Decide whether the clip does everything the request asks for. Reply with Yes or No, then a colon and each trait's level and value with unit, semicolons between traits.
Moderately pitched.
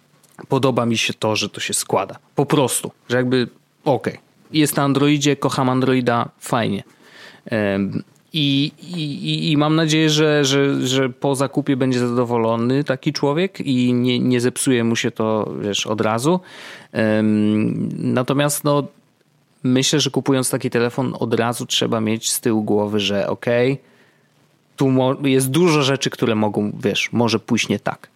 No: low, 130 Hz